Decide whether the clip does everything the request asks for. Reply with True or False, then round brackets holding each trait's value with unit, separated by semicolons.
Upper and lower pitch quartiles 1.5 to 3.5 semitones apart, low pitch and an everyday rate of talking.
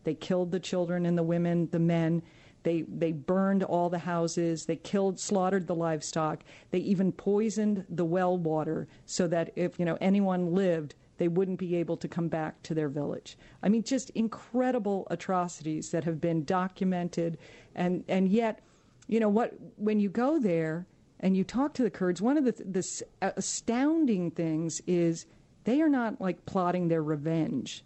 False (2.8 semitones; 180 Hz; 175 wpm)